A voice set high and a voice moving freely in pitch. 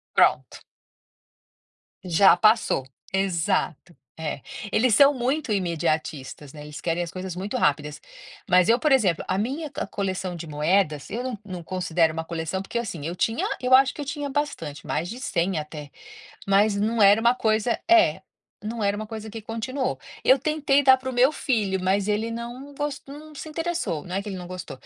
Yes: high, 205 Hz; wide, 6.6 semitones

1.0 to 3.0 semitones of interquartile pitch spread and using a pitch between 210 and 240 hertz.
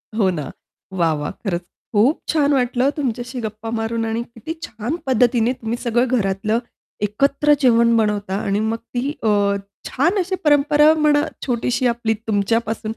No: average, 3.7 semitones; high, 235 Hz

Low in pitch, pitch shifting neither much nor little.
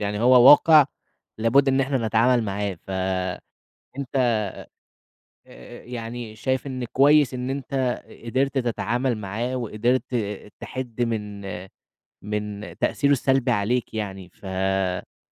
Yes: low, 120 Hz; average, 3.9 semitones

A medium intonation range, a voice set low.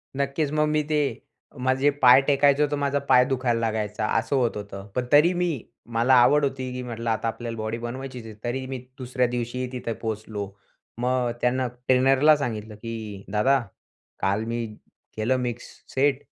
Yes: average, 3.0 semitones; low, 125 Hz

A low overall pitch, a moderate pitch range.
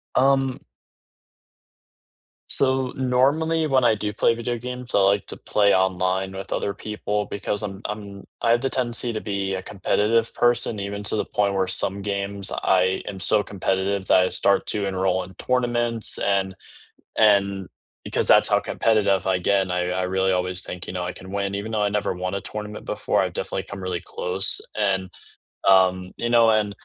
Yes: low, 100 Hz; average, 3.1 semitones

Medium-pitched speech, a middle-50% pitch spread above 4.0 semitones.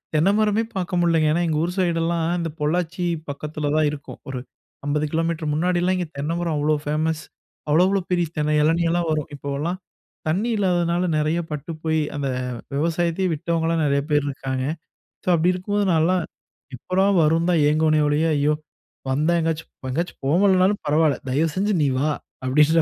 No: medium, 160 Hz; narrow, 2.6 semitones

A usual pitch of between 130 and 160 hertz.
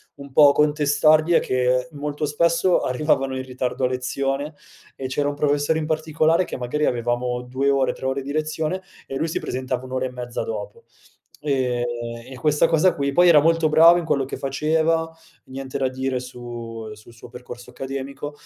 Yes: medium, 140 Hz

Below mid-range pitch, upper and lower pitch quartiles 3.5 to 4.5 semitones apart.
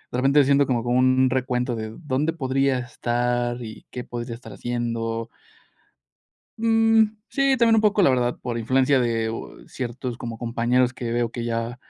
No: low, 125 Hz; narrow, 2.5 semitones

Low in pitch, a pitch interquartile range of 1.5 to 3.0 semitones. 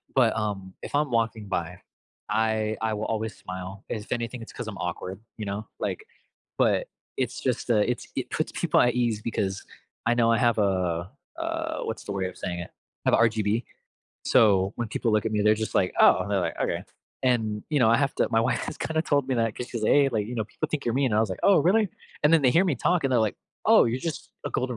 No: low, 115 Hz; average, 3.4 semitones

